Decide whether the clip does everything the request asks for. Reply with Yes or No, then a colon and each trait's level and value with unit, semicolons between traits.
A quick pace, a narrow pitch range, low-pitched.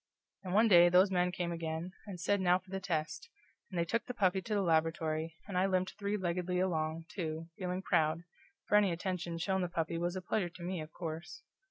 No: fast, 225 wpm; narrow, 2.3 semitones; medium, 180 Hz